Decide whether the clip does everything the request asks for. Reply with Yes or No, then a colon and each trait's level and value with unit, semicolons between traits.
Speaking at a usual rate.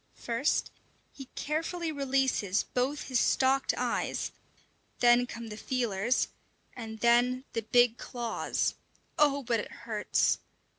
No: slow, 115 wpm